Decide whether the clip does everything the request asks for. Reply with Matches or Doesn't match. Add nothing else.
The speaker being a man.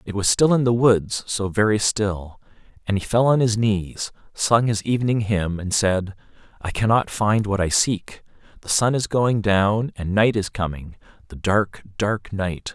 Matches